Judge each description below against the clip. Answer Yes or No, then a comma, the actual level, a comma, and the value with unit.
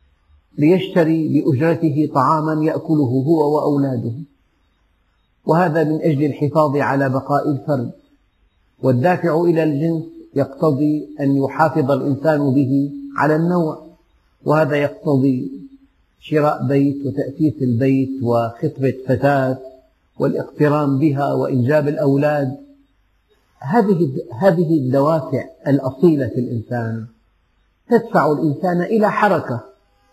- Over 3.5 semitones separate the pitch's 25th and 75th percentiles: No, average, 3.2 semitones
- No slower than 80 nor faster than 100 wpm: Yes, average, 90 wpm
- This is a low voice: No, medium, 145 Hz